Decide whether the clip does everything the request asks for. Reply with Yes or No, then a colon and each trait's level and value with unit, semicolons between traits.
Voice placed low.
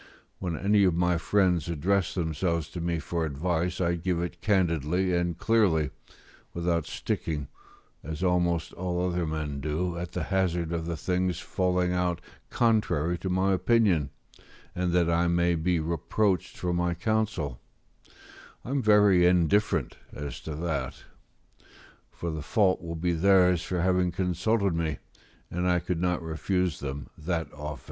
Yes: very low, 85 Hz